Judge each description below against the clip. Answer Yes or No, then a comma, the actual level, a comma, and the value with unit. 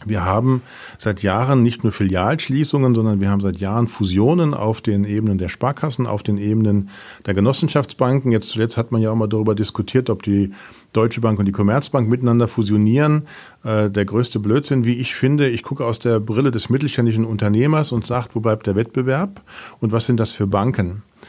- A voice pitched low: Yes, low, 115 Hz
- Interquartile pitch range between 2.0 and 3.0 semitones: No, average, 3.5 semitones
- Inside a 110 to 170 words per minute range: No, fast, 190 wpm